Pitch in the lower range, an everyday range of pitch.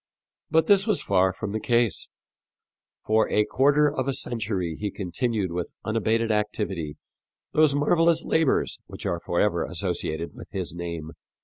No: low, 110 Hz; wide, 7.1 semitones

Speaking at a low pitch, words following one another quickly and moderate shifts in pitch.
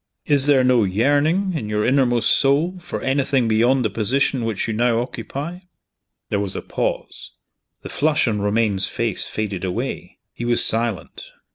No: low, 120 Hz; average, 160 wpm; average, 4.3 semitones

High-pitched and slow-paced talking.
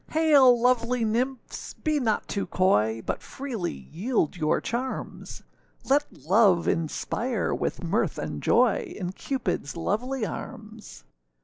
Yes: high, 230 Hz; slow, 120 wpm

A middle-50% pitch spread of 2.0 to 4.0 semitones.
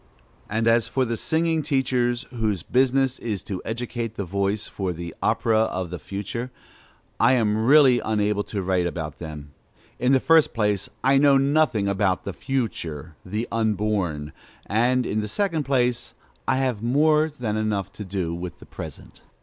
No: average, 4.7 semitones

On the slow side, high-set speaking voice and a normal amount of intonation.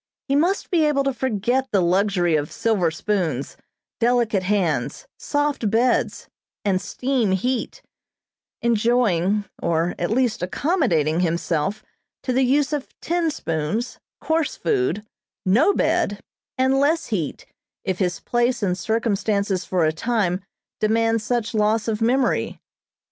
No: slow, 130 wpm; high, 220 Hz; wide, 5.8 semitones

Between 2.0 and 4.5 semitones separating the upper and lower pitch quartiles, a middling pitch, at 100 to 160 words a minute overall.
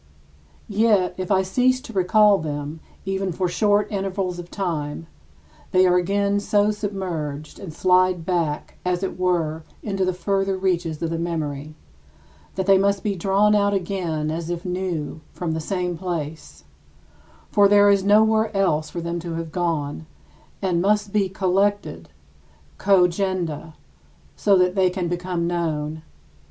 Yes: average, 3.0 semitones; medium, 180 Hz; average, 150 wpm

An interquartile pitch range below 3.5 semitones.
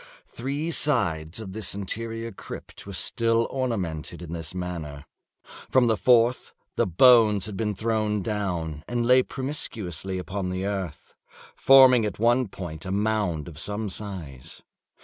No: average, 4.7 semitones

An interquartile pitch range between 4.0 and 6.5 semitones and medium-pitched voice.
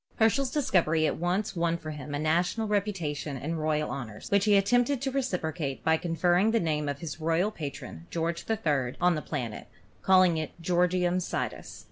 Yes: average, 4.4 semitones; medium, 170 Hz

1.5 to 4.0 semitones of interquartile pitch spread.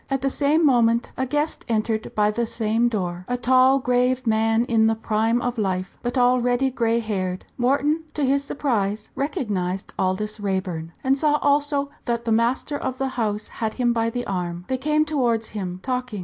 Yes: average, 3.6 semitones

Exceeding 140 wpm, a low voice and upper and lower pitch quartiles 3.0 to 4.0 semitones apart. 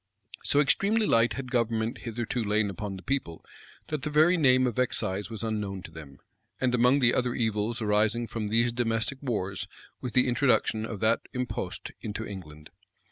Yes: average, 175 wpm; low, 115 Hz; average, 3.4 semitones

